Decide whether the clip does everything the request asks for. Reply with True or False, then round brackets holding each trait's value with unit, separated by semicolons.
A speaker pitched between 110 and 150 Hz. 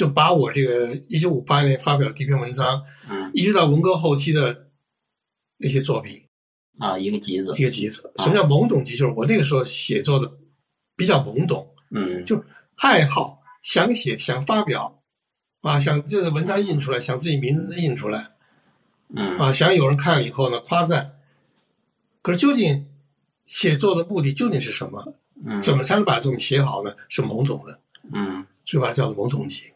True (140 Hz)